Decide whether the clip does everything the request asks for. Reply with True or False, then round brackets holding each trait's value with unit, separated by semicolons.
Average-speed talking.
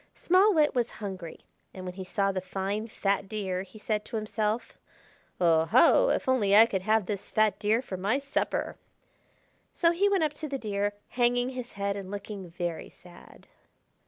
True (180 wpm)